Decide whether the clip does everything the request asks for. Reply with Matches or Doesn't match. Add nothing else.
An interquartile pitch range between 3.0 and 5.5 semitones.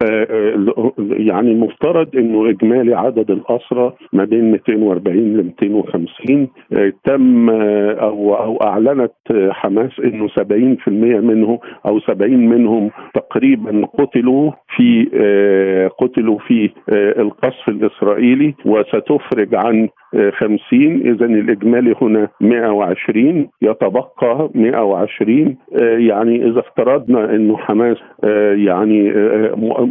Doesn't match